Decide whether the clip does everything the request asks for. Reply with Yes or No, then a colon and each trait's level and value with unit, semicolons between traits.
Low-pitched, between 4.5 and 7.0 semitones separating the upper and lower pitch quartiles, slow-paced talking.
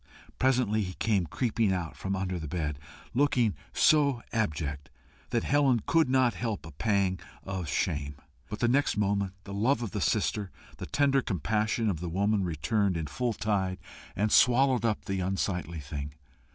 No: low, 100 Hz; average, 4.9 semitones; average, 165 wpm